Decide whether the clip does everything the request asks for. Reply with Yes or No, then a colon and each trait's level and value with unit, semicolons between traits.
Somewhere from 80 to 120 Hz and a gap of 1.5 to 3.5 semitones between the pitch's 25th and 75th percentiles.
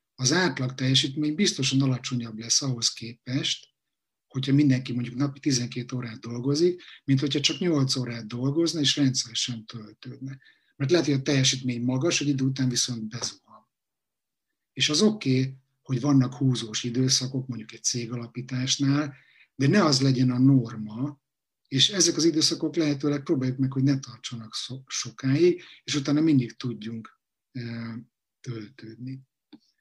No: low, 130 Hz; average, 2.9 semitones